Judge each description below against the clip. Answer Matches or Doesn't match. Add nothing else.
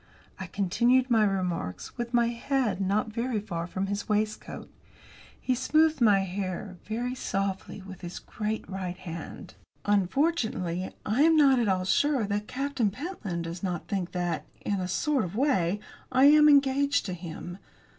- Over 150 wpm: Matches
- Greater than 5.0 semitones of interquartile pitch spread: Matches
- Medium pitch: Doesn't match